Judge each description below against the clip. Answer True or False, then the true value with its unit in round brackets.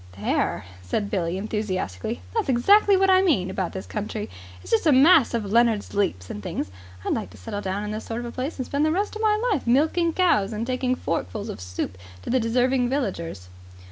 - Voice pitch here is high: True (230 Hz)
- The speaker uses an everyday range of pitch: False (6.8 semitones)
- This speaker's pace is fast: True (210 wpm)